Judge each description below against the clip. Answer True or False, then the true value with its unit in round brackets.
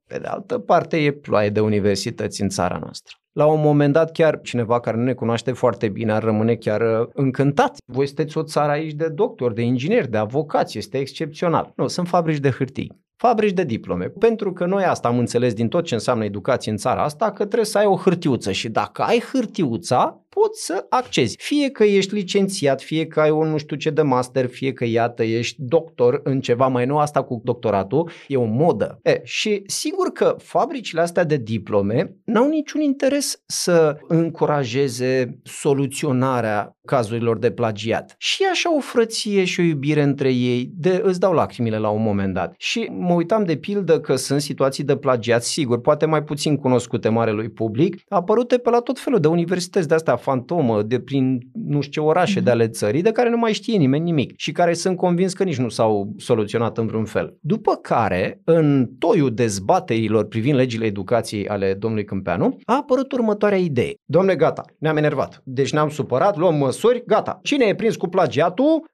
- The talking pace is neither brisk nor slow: False (195 wpm)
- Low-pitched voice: False (150 Hz)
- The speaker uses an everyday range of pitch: False (7.6 semitones)